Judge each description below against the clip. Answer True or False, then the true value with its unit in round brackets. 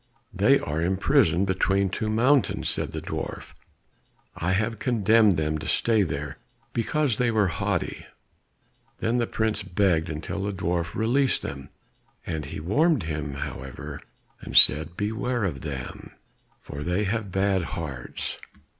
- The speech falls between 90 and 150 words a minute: True (145 wpm)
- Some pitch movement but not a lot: False (5.7 semitones)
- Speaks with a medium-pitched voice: False (95 Hz)